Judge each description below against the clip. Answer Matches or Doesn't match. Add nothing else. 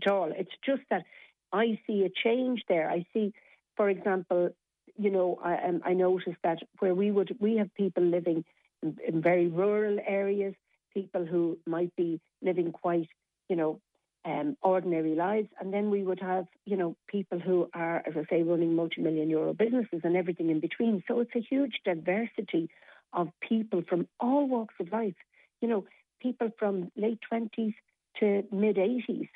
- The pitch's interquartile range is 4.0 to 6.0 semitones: Doesn't match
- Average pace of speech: Matches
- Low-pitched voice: Doesn't match